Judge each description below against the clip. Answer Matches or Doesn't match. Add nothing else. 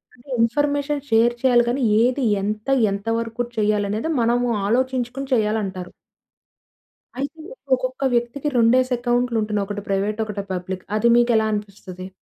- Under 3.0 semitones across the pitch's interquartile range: Doesn't match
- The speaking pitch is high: Matches